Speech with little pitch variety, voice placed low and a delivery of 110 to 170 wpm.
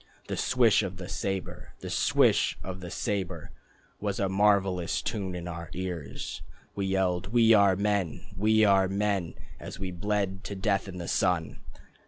Yes: narrow, 2.0 semitones; very low, 95 Hz; average, 165 wpm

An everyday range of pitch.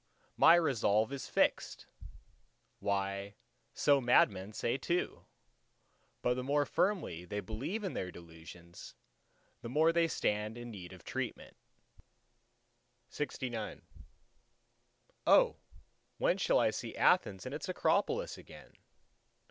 No: wide, 7.8 semitones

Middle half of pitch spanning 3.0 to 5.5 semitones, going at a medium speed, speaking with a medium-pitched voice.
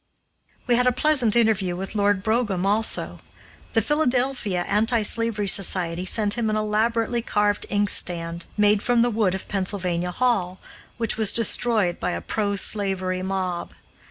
No: average, 3.6 semitones; average, 150 wpm; high, 210 Hz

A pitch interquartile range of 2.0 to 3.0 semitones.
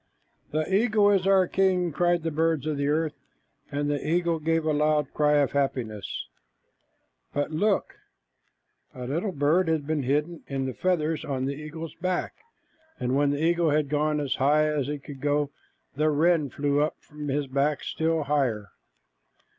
Yes: narrow, 2.4 semitones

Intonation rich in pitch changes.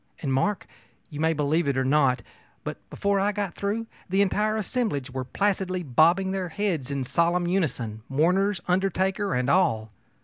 Yes: wide, 5.9 semitones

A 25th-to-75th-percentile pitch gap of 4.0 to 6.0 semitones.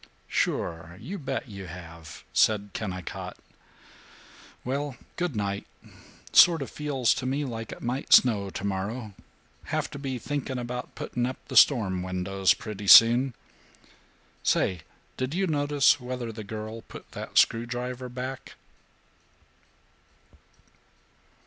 Yes: average, 4.9 semitones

